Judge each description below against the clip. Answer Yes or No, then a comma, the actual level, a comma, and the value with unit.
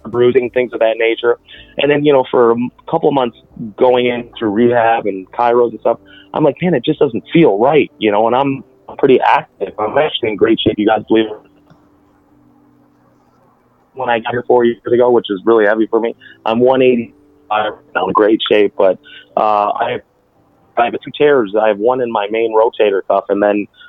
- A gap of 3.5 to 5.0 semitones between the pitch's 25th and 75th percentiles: No, average, 2.8 semitones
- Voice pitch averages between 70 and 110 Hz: No, low, 120 Hz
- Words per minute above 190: Yes, fast, 205 wpm